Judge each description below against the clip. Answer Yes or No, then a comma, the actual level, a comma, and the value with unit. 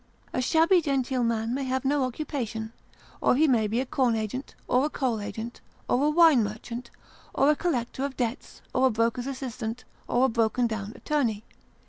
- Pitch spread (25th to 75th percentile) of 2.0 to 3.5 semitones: Yes, average, 3.2 semitones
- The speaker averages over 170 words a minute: Yes, average, 185 wpm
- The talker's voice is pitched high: Yes, very high, 250 Hz